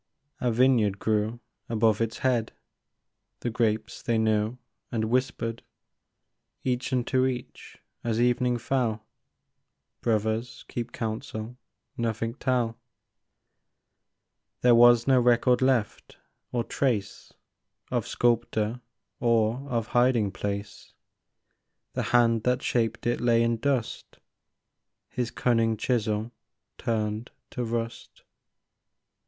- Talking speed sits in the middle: No, slow, 105 wpm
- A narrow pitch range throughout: Yes, narrow, 1.9 semitones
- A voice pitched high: No, low, 115 Hz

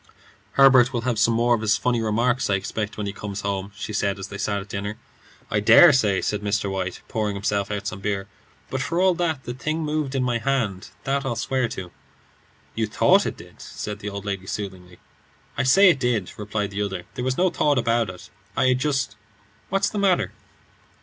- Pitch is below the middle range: Yes, low, 110 Hz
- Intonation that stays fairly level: No, average, 4.7 semitones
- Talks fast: Yes, fast, 215 wpm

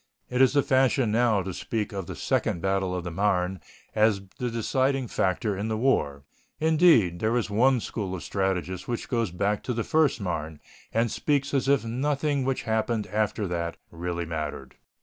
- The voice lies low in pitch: Yes, low, 110 Hz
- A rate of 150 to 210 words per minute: Yes, average, 185 wpm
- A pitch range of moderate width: No, wide, 5.7 semitones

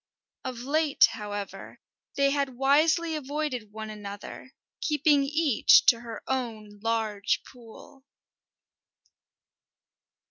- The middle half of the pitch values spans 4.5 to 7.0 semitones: Yes, average, 4.9 semitones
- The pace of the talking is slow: Yes, slow, 95 wpm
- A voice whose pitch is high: Yes, very high, 255 Hz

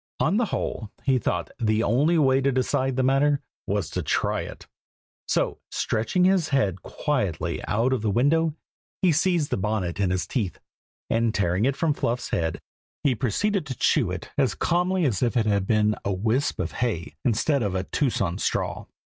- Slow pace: No, average, 185 wpm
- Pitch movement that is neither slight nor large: No, wide, 6.2 semitones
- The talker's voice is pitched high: No, low, 120 Hz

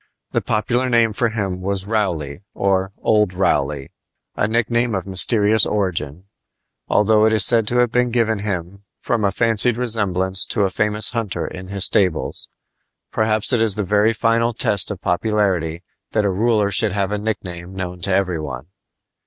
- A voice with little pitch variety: No, average, 3.1 semitones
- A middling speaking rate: Yes, average, 170 wpm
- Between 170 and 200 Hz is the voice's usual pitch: No, low, 105 Hz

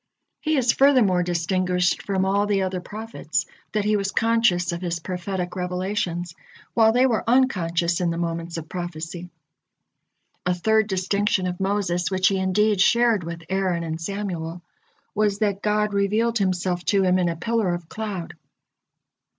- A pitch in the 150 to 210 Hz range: Yes, high, 190 Hz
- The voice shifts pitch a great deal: No, average, 3.0 semitones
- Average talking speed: Yes, average, 160 wpm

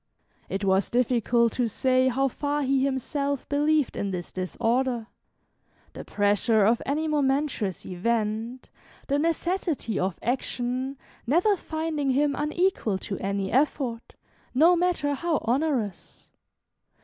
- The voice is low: No, very high, 260 Hz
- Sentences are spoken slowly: Yes, slow, 120 wpm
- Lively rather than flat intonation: No, average, 4.7 semitones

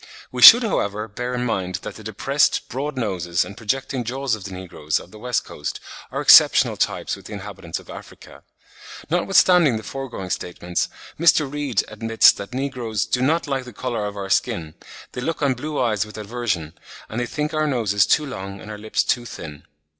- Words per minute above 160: Yes, average, 195 wpm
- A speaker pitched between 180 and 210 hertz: No, low, 115 Hz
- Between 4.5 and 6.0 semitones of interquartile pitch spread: Yes, average, 5.0 semitones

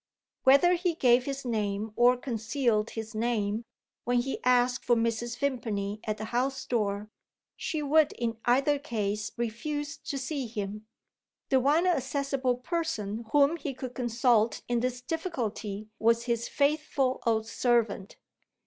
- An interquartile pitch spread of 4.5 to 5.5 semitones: No, average, 3.7 semitones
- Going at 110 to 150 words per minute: Yes, average, 140 wpm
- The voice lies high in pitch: Yes, high, 245 Hz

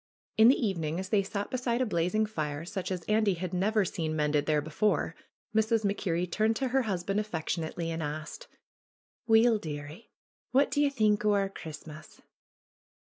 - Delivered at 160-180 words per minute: Yes, average, 175 wpm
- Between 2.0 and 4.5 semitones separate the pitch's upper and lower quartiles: No, average, 5.1 semitones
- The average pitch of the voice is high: Yes, high, 195 Hz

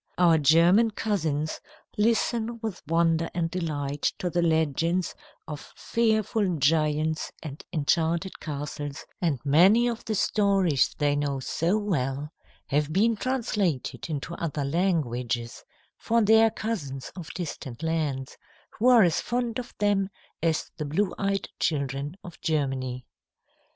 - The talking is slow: Yes, slow, 130 wpm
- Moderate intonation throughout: No, wide, 5.7 semitones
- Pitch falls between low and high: Yes, medium, 165 Hz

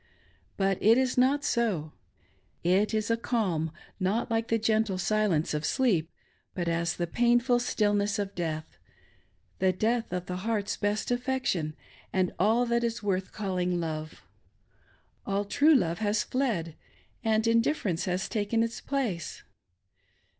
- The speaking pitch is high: Yes, high, 205 Hz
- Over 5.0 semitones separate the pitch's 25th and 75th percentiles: No, average, 4.3 semitones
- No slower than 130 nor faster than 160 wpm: Yes, average, 145 wpm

